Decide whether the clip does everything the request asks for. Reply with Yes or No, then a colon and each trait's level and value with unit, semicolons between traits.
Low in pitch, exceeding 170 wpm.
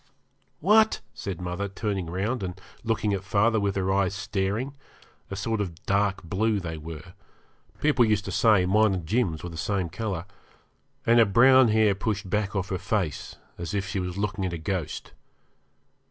Yes: low, 100 Hz; average, 180 wpm